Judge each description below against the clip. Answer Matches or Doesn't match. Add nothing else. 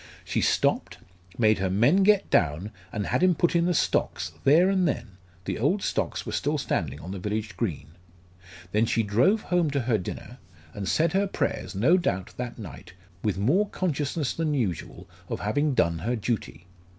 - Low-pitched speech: Matches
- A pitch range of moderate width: Doesn't match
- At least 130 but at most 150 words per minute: Doesn't match